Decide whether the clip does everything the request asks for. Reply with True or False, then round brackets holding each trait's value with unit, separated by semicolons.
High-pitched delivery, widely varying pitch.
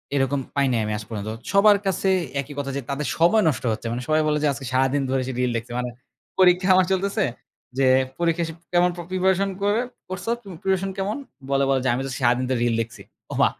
False (150 Hz; 6.5 semitones)